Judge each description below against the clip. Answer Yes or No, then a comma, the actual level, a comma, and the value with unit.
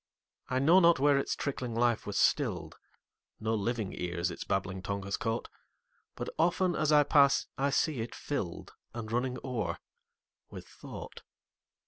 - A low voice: Yes, low, 120 Hz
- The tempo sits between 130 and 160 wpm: Yes, average, 140 wpm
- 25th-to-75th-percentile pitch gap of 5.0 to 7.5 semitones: Yes, wide, 5.6 semitones